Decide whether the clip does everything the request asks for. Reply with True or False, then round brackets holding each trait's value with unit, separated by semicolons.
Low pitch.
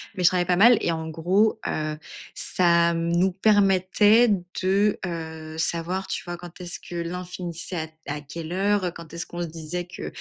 False (175 Hz)